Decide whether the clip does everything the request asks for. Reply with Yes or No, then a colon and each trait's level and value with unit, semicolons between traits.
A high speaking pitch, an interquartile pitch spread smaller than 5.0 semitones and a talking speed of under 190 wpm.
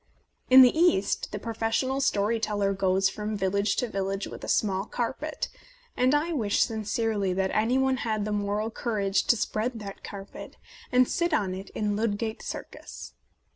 Yes: high, 215 Hz; average, 3.3 semitones; average, 170 wpm